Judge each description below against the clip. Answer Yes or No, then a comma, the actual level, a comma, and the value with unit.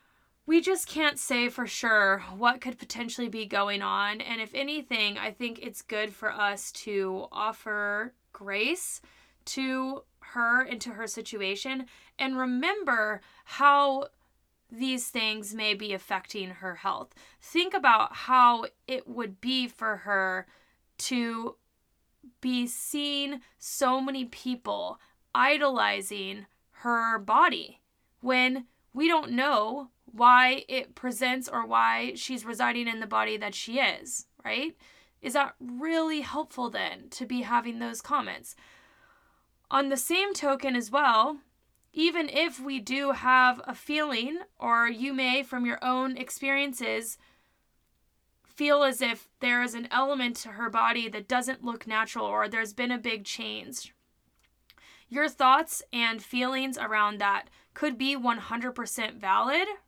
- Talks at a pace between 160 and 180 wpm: No, slow, 135 wpm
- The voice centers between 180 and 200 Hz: No, very high, 250 Hz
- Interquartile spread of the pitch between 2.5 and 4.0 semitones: Yes, average, 3.6 semitones